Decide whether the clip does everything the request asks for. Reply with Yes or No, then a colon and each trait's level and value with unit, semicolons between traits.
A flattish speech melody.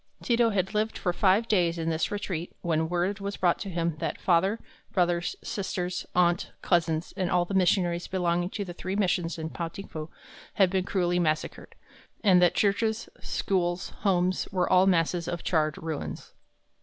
Yes: narrow, 2.2 semitones